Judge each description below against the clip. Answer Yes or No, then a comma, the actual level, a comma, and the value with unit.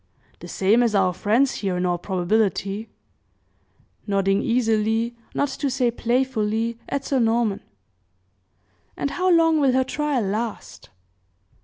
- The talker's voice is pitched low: No, high, 230 Hz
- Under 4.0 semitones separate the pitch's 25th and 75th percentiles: No, average, 4.5 semitones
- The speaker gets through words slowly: Yes, slow, 130 wpm